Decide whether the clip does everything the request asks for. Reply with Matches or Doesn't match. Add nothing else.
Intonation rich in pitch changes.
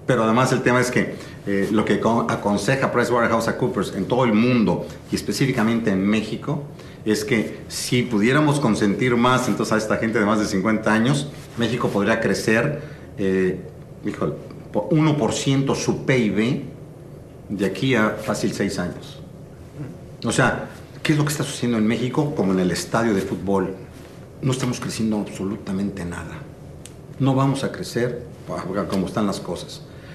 Doesn't match